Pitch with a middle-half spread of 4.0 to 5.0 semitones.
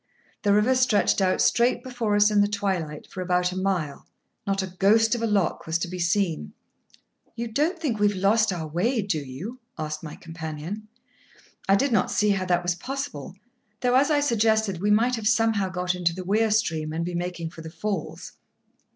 Yes: average, 4.3 semitones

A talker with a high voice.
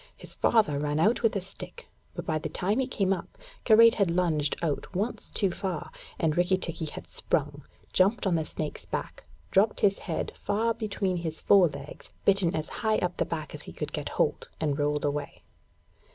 No: medium, 180 Hz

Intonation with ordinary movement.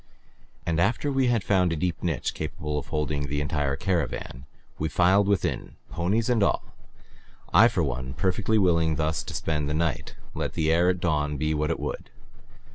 Yes: average, 3.9 semitones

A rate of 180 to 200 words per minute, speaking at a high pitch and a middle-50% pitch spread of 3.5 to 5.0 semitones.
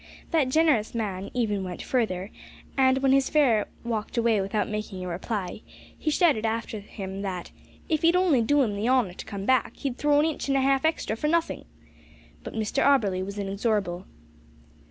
No: average, 190 wpm; high, 225 Hz; wide, 5.4 semitones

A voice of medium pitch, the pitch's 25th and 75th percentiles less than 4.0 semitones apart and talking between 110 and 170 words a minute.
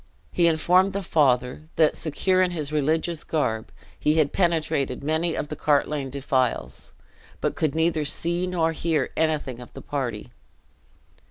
Yes: medium, 155 Hz; average, 3.0 semitones; average, 150 wpm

